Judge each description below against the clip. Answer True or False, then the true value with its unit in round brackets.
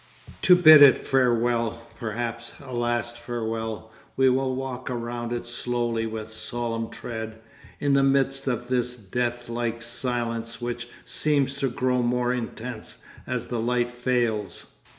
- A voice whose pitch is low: True (120 Hz)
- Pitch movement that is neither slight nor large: False (1.4 semitones)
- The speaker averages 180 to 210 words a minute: False (135 wpm)